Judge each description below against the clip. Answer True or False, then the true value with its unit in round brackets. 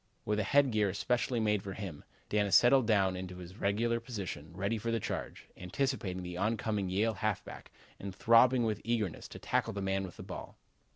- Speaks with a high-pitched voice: False (105 Hz)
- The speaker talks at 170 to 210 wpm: True (190 wpm)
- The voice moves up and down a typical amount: True (3.3 semitones)